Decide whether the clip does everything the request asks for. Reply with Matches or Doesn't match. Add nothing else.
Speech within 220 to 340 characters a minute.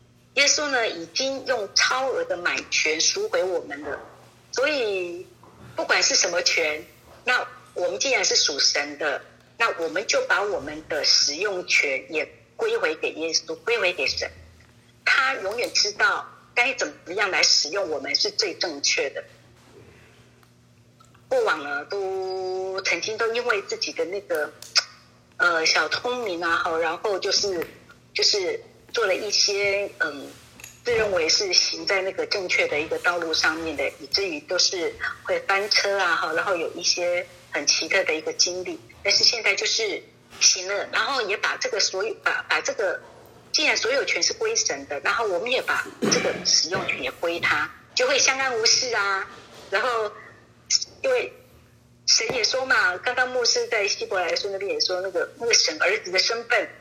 Matches